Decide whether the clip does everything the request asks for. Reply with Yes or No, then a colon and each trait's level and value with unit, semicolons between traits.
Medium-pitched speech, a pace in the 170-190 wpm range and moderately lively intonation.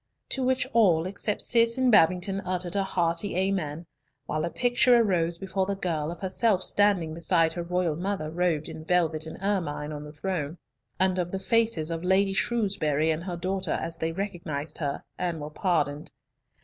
Yes: medium, 180 Hz; average, 180 wpm; average, 3.4 semitones